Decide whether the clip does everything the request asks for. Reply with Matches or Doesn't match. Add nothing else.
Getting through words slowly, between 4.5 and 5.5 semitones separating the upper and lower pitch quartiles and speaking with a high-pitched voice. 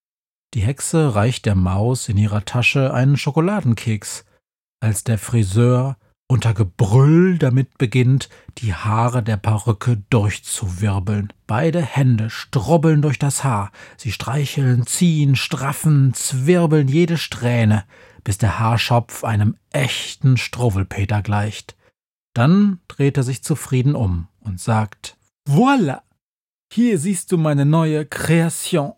Doesn't match